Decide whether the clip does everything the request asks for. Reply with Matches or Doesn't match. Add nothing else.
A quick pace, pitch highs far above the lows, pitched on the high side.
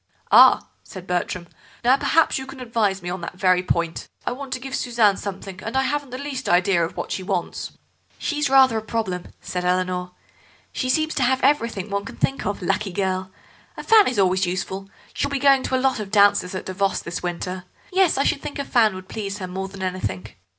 Matches